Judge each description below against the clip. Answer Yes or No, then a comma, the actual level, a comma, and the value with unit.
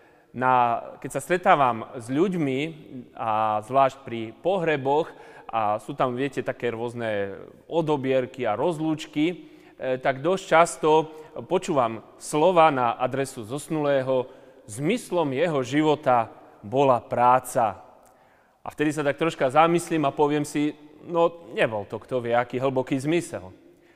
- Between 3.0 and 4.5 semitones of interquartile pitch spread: Yes, average, 3.9 semitones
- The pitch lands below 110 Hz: No, low, 135 Hz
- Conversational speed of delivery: Yes, average, 125 wpm